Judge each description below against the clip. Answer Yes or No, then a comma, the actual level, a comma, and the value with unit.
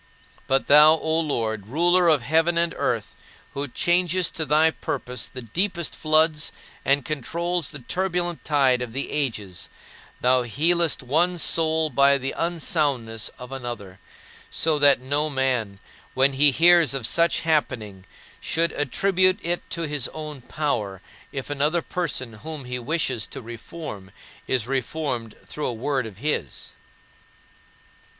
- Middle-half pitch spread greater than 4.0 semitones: Yes, average, 4.6 semitones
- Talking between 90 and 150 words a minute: Yes, average, 145 wpm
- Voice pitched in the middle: Yes, medium, 145 Hz